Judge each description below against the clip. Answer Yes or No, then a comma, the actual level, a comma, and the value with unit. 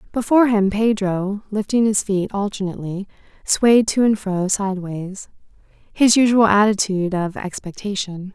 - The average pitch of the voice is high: Yes, high, 205 Hz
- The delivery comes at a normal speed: No, slow, 115 wpm